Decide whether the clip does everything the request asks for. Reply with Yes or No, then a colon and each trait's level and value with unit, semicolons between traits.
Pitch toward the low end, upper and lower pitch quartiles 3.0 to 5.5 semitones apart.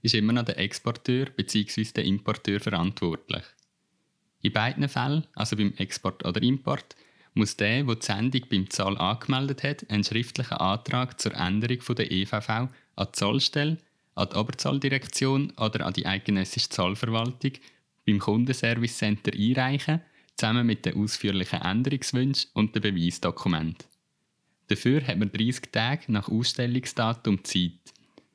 Yes: low, 115 Hz; average, 4.2 semitones